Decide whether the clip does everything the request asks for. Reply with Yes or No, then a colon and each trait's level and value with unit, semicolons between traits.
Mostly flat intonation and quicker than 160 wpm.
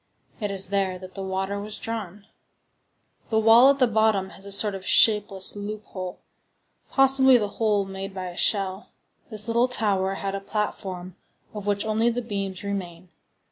Yes: narrow, 2.3 semitones; average, 170 wpm